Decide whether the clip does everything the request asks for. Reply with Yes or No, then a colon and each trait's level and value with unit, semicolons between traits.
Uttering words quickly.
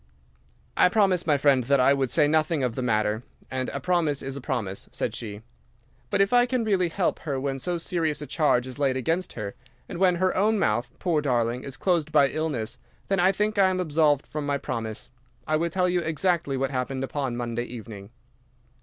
Yes: fast, 210 wpm